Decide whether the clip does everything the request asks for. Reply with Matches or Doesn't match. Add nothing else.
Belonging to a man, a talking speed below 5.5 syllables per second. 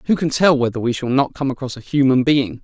Doesn't match